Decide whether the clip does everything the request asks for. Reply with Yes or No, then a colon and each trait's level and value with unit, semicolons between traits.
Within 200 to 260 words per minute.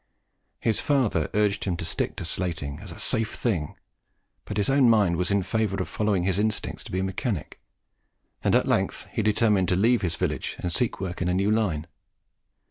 Yes: fast, 205 wpm